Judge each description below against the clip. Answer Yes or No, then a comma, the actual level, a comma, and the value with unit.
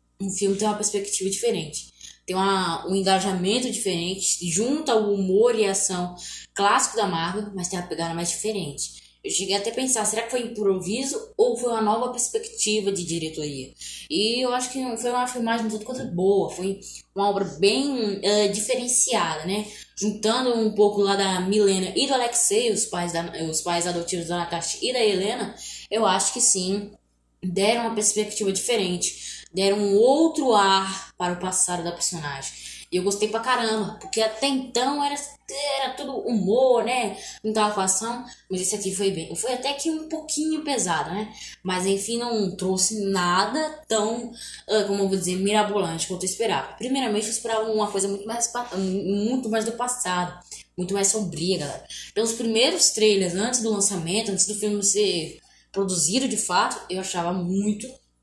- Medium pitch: No, high, 205 Hz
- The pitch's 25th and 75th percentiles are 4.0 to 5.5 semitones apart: No, average, 3.6 semitones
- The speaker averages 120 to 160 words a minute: No, average, 175 wpm